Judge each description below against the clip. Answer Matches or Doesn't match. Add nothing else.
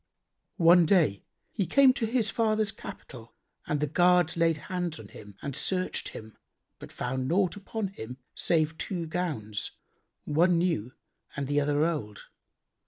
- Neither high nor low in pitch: Matches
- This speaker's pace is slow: Doesn't match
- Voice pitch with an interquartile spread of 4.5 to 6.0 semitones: Matches